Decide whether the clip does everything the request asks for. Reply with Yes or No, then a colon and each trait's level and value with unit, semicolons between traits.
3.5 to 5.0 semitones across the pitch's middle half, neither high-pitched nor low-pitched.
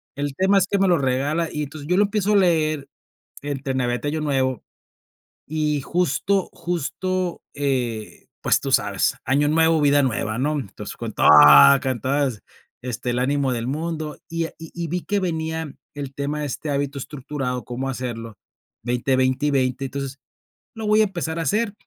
Yes: average, 4.0 semitones; medium, 145 Hz